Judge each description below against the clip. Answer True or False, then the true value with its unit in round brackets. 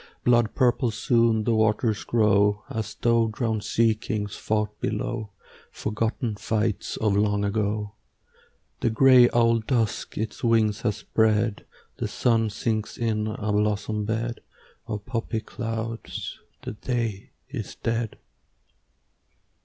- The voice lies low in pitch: True (110 Hz)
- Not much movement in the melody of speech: True (1.6 semitones)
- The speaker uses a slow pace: True (120 wpm)